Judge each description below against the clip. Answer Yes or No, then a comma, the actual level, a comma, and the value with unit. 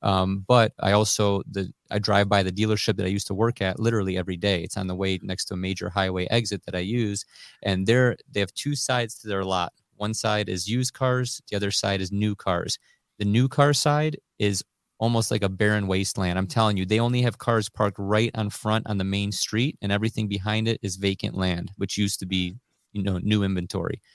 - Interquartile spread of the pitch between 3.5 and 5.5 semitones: No, narrow, 2.5 semitones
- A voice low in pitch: Yes, low, 105 Hz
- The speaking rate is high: Yes, fast, 230 wpm